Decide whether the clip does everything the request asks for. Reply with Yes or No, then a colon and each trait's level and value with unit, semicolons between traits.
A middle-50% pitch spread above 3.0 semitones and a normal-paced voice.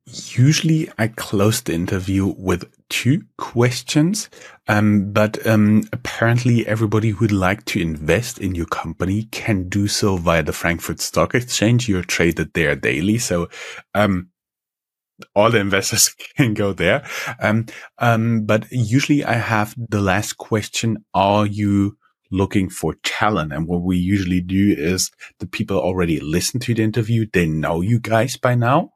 Yes: average, 3.5 semitones; average, 155 wpm